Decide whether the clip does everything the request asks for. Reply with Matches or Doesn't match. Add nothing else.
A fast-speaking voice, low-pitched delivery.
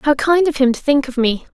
Doesn't match